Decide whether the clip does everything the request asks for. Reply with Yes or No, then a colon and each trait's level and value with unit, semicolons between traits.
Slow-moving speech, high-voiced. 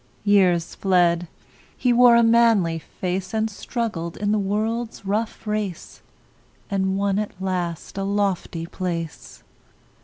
Yes: slow, 125 wpm; high, 195 Hz